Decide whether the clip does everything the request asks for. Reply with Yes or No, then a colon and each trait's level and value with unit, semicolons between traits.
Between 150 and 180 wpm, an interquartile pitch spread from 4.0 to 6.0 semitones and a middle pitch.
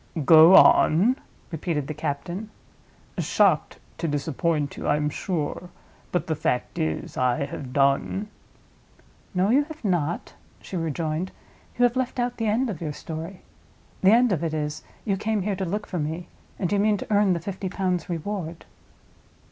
Yes: average, 170 wpm; average, 4.9 semitones; medium, 175 Hz